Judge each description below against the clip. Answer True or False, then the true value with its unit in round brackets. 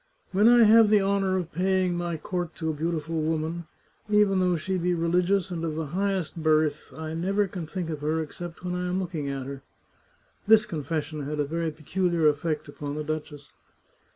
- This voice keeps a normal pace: False (210 wpm)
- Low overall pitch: False (170 Hz)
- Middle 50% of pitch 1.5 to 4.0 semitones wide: True (3.2 semitones)